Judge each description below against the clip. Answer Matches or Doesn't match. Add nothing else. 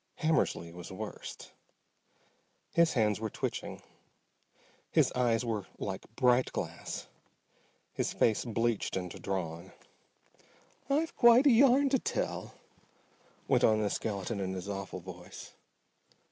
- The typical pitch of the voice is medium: Doesn't match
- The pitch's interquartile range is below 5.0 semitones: Doesn't match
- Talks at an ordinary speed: Doesn't match